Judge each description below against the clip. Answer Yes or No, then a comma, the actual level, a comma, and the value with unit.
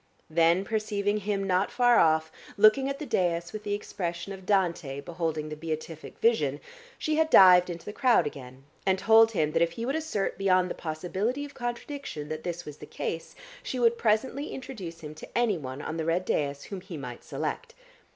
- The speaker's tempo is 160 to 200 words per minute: Yes, average, 195 wpm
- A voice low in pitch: No, medium, 185 Hz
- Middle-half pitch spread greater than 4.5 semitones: Yes, wide, 5.6 semitones